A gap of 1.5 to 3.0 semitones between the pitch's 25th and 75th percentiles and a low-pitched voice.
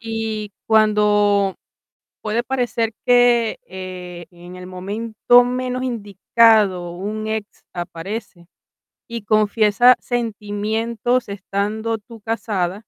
No: narrow, 2.6 semitones; high, 215 Hz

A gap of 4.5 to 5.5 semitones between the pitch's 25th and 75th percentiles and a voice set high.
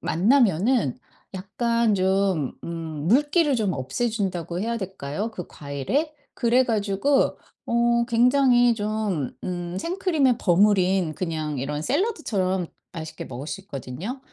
No: wide, 5.9 semitones; high, 200 Hz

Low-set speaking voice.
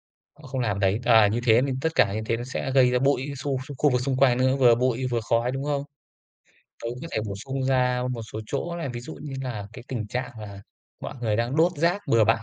Yes: low, 125 Hz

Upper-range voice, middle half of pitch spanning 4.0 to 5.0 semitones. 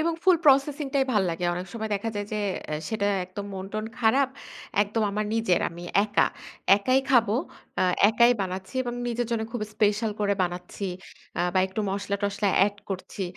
No: high, 210 Hz; average, 3.1 semitones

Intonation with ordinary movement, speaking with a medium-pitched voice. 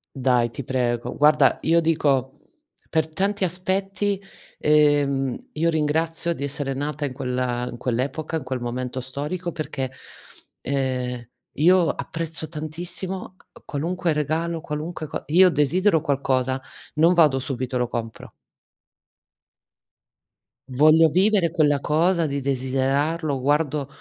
Yes: average, 3.9 semitones; medium, 150 Hz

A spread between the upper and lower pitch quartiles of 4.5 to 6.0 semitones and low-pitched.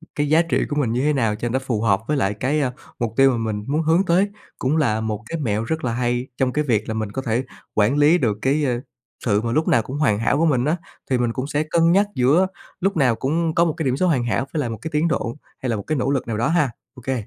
Yes: average, 5.0 semitones; low, 130 Hz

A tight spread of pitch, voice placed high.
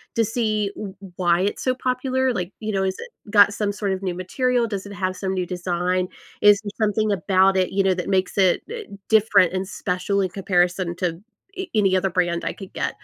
Yes: narrow, 2.3 semitones; high, 195 Hz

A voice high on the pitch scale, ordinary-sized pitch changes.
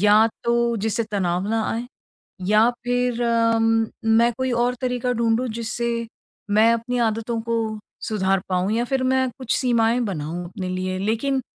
No: high, 230 Hz; narrow, 2.2 semitones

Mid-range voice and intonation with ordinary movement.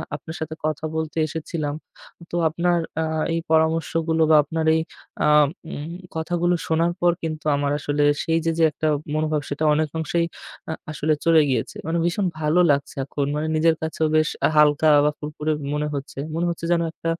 No: medium, 160 Hz; narrow, 1.5 semitones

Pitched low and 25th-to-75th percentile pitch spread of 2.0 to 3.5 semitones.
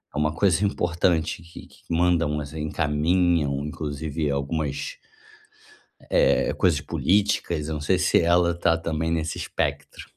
Yes: very low, 80 Hz; narrow, 2.6 semitones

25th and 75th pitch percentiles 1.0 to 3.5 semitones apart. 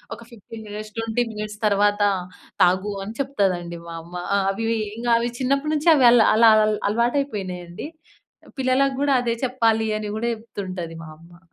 No: average, 3.9 semitones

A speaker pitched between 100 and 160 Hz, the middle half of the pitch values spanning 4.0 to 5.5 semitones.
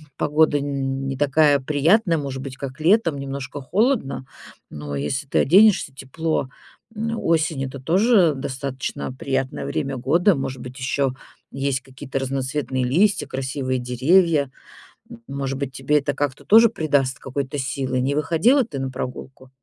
No: medium, 140 Hz; average, 3.1 semitones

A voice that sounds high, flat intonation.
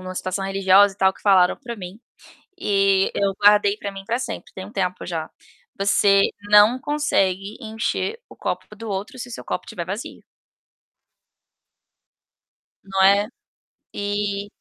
Yes: high, 200 Hz; narrow, 1.5 semitones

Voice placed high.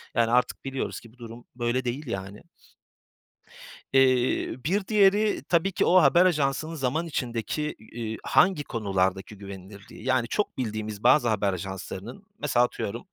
No: low, 125 Hz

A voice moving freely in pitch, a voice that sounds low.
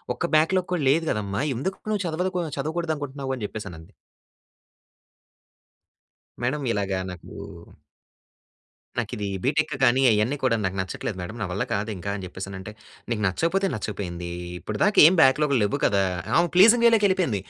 Yes: wide, 8.9 semitones; low, 130 Hz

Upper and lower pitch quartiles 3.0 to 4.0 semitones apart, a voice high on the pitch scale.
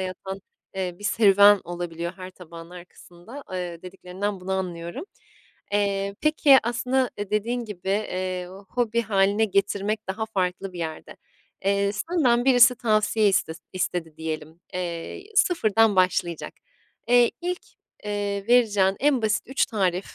Yes: average, 3.6 semitones; high, 200 Hz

